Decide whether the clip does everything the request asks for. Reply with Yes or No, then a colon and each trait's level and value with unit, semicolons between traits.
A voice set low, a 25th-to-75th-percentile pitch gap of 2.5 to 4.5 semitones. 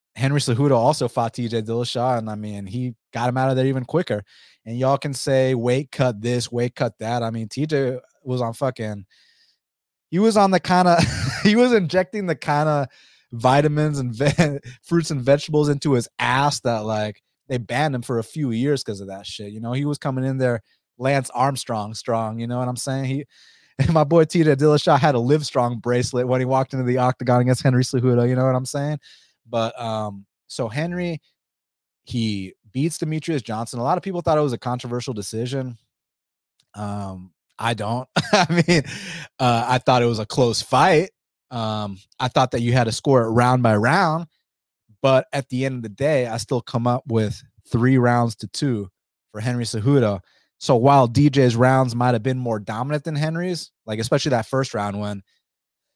Yes: low, 125 Hz; average, 3.6 semitones